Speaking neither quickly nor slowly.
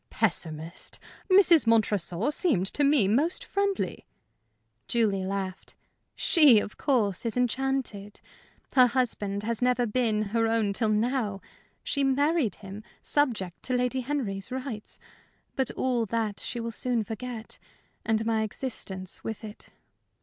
No: slow, 130 wpm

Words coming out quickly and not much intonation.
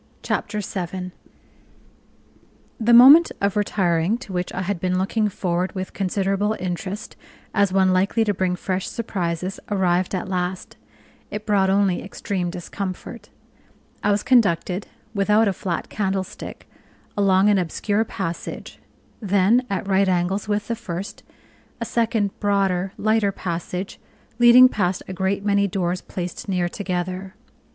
No: slow, 135 wpm; narrow, 2.1 semitones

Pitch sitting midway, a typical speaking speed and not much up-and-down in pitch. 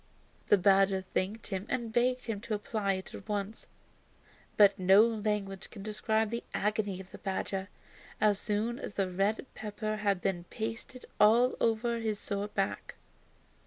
No: high, 210 Hz; average, 160 wpm; narrow, 2.3 semitones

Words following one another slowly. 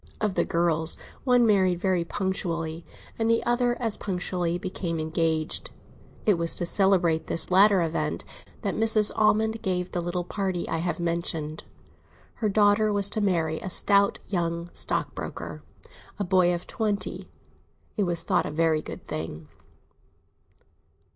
No: average, 145 wpm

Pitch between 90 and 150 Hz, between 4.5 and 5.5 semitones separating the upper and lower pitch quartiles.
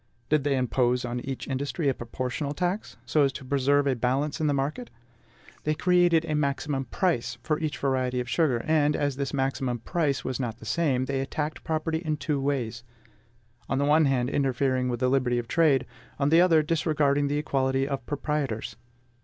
No: medium, 140 Hz; average, 2.9 semitones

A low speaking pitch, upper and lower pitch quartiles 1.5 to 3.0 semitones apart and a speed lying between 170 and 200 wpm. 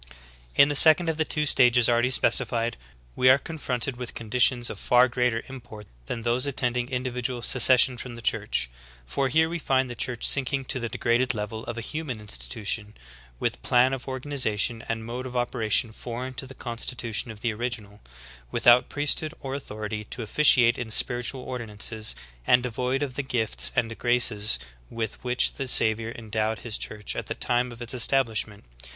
Yes: low, 120 Hz; narrow, 2.4 semitones; average, 180 wpm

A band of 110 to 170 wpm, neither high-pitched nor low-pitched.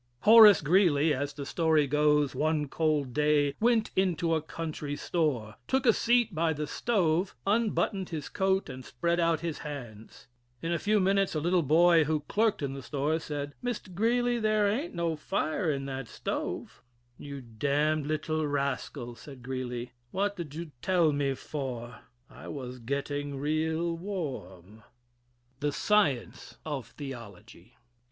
Yes: average, 155 wpm; medium, 155 Hz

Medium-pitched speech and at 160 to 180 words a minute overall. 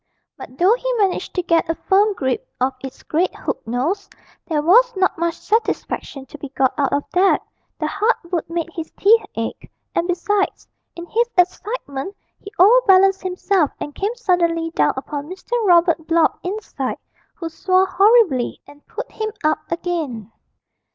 No: very high, 350 Hz; average, 165 wpm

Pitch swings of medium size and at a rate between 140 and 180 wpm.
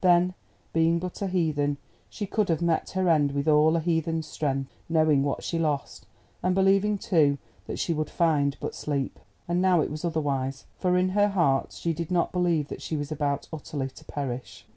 No: average, 3.6 semitones; average, 200 wpm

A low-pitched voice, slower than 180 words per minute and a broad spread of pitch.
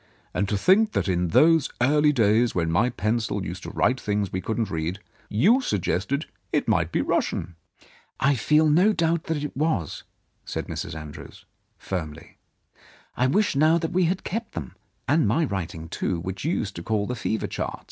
No: low, 115 Hz; average, 190 wpm; wide, 9.0 semitones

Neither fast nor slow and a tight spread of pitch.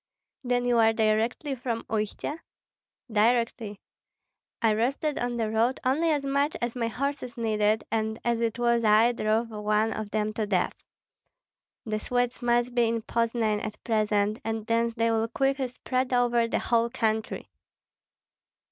Yes: average, 155 wpm; narrow, 2.0 semitones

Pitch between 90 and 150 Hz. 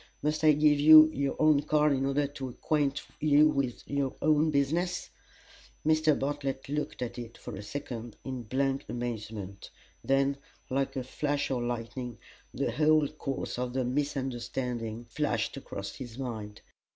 Yes: low, 135 Hz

